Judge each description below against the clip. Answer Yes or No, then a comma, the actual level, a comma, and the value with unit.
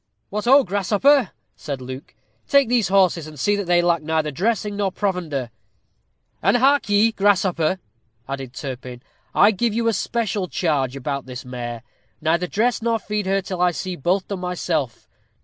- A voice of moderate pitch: Yes, medium, 180 Hz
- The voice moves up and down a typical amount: No, wide, 5.8 semitones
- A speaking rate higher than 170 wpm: No, average, 165 wpm